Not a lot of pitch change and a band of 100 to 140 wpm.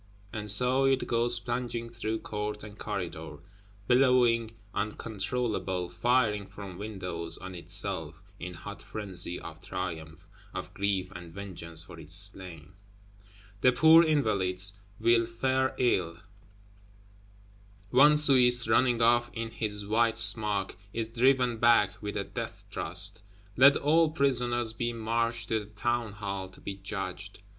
No: average, 4.1 semitones; slow, 135 wpm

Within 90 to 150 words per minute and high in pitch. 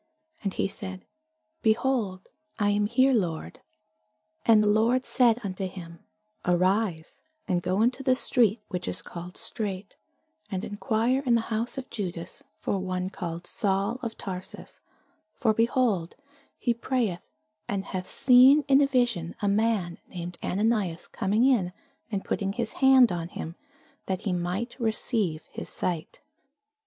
Yes: average, 145 wpm; high, 205 Hz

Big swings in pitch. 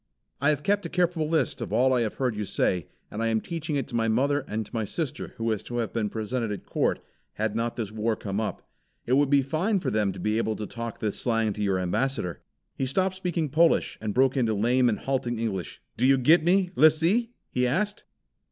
Yes: wide, 5.7 semitones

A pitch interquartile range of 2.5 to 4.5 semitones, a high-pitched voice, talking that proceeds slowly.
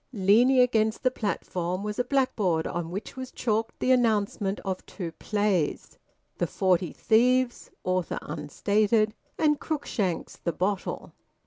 No: average, 5.0 semitones; high, 210 Hz; slow, 130 wpm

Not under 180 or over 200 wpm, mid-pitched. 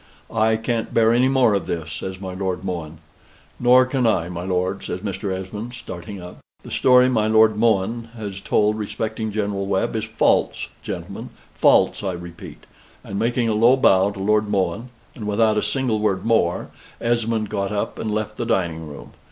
No: average, 185 wpm; low, 105 Hz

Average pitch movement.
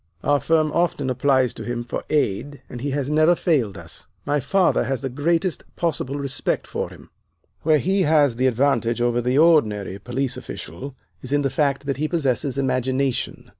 Yes: average, 3.2 semitones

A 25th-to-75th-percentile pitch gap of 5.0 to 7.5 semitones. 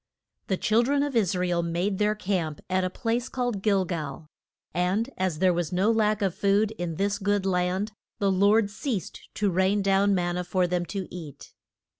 No: average, 2.7 semitones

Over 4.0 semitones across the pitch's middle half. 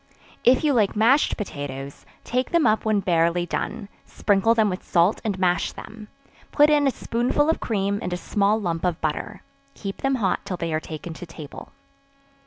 Yes: average, 4.8 semitones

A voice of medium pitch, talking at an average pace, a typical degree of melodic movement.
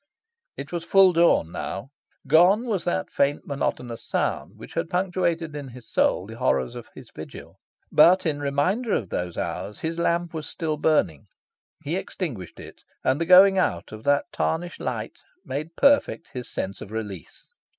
No: medium, 160 Hz; average, 170 wpm; wide, 5.9 semitones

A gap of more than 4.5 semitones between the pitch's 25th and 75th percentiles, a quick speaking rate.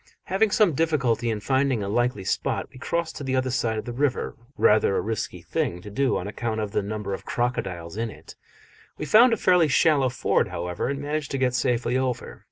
Yes: average, 5.0 semitones; fast, 215 wpm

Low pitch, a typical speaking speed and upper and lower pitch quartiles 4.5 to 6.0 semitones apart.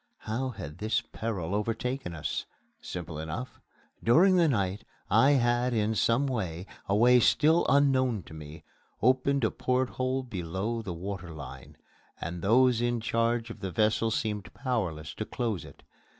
Yes: low, 115 Hz; average, 150 wpm; average, 5.3 semitones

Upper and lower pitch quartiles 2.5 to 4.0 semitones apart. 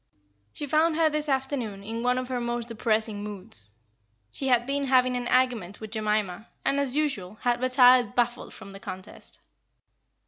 Yes: average, 3.5 semitones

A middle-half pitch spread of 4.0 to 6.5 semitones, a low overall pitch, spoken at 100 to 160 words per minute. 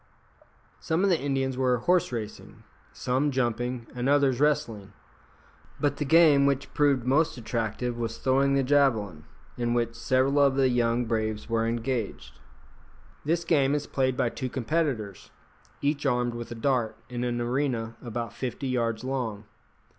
No: average, 3.1 semitones; low, 125 Hz; average, 155 wpm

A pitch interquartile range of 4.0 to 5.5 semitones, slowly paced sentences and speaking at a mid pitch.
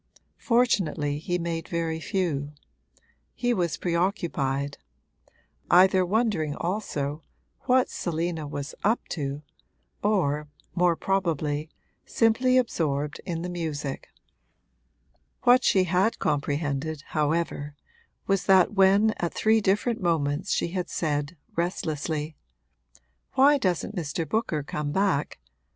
Yes: average, 4.6 semitones; slow, 105 wpm; medium, 170 Hz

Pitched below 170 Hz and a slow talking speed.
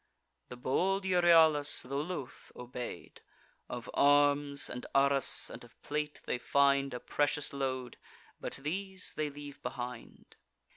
Yes: medium, 140 Hz; slow, 130 wpm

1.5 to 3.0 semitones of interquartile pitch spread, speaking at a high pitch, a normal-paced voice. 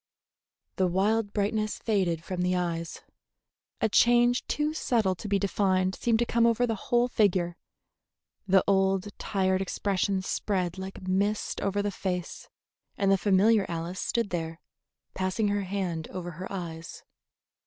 Yes: narrow, 2.6 semitones; high, 195 Hz; average, 145 wpm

